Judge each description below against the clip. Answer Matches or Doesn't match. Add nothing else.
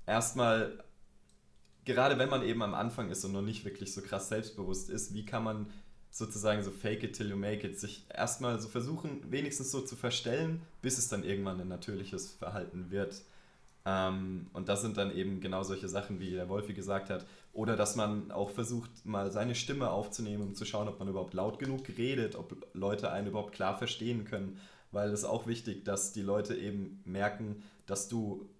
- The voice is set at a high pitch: Doesn't match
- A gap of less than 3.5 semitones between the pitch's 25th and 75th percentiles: Matches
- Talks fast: Matches